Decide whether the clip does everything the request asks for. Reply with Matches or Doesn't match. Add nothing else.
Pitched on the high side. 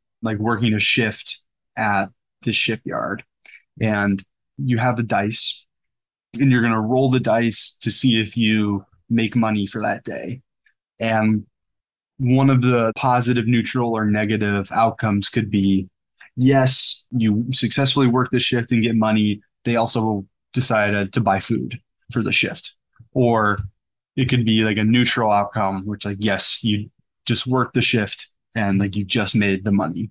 Doesn't match